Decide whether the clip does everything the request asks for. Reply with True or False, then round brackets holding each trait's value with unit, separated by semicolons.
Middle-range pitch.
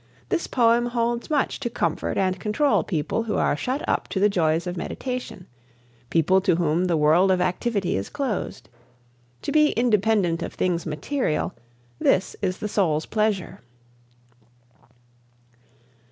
False (195 Hz)